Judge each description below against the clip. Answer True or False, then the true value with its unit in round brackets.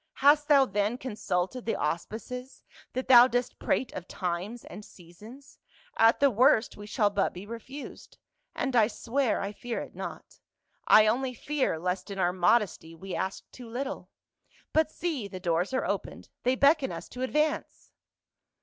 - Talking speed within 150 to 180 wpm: True (165 wpm)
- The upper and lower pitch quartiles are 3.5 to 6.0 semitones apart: True (5.1 semitones)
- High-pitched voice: True (230 Hz)